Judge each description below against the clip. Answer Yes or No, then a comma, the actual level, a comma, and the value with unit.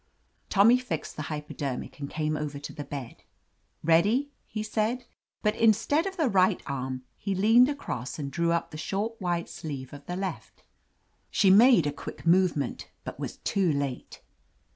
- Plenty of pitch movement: Yes, wide, 6.8 semitones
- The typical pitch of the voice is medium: Yes, medium, 175 Hz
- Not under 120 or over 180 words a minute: Yes, average, 170 wpm